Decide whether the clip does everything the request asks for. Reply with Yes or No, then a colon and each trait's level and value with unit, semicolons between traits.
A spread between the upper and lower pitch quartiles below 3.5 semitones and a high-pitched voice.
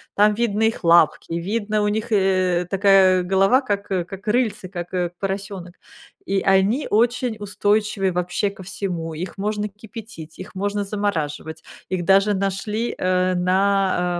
Yes: narrow, 2.4 semitones; high, 195 Hz